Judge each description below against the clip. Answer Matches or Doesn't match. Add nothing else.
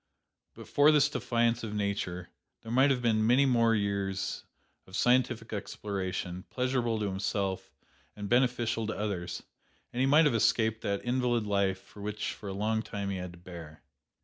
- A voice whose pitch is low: Matches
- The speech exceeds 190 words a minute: Doesn't match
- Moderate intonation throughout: Matches